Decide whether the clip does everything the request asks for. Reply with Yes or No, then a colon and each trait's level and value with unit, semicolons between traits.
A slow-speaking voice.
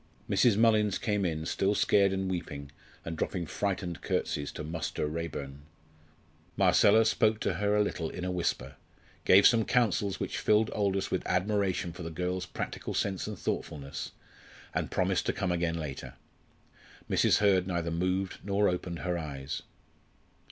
No: average, 155 wpm